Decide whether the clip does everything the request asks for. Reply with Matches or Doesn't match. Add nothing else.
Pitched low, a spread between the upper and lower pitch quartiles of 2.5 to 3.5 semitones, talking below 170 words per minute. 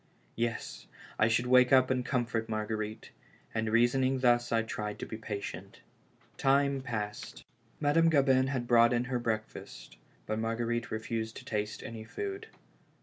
Matches